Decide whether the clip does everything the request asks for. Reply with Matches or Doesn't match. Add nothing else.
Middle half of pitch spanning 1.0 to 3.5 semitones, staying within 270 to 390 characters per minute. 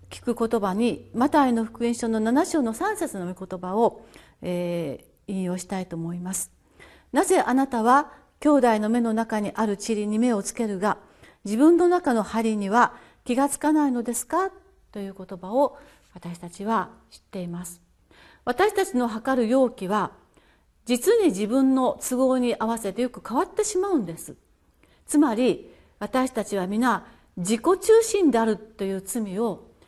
Doesn't match